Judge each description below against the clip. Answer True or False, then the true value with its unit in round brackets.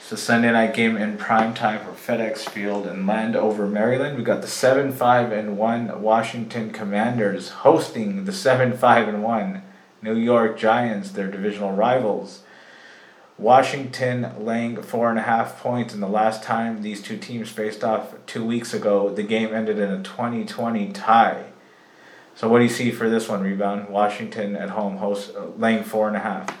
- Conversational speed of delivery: True (185 wpm)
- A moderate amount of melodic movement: False (2.1 semitones)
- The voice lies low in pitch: True (110 Hz)